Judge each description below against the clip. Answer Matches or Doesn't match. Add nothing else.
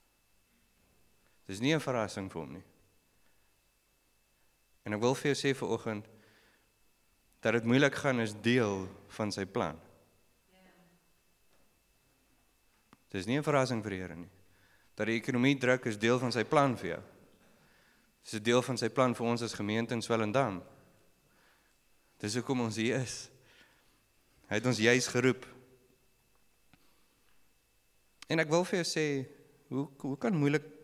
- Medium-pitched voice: Doesn't match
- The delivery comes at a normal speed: Matches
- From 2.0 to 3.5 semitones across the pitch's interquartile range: Doesn't match